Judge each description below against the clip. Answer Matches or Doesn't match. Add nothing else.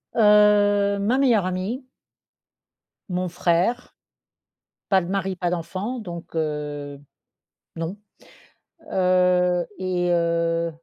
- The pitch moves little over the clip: Doesn't match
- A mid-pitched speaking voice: Matches